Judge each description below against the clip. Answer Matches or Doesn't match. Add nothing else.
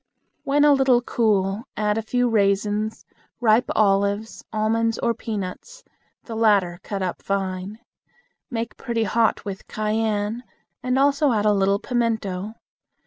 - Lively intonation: Doesn't match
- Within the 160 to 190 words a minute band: Doesn't match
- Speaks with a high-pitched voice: Matches